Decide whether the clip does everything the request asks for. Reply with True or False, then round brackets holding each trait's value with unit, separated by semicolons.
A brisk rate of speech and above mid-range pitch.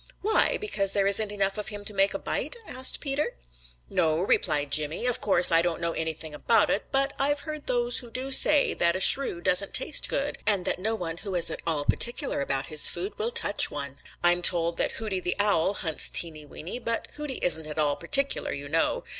True (220 wpm; 195 Hz)